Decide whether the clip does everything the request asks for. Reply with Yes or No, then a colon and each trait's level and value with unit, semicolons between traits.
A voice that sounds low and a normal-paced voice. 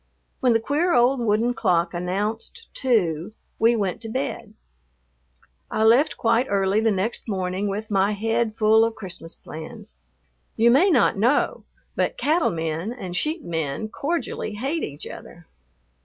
No: high, 220 Hz; average, 150 wpm